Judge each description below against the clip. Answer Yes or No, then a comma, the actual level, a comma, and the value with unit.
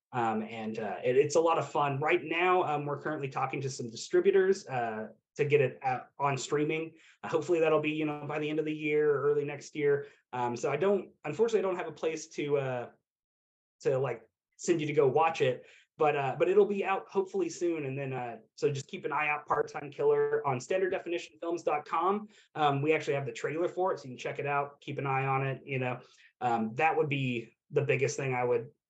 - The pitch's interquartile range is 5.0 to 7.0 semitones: Yes, wide, 5.4 semitones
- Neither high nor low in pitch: Yes, medium, 155 Hz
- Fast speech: Yes, fast, 235 wpm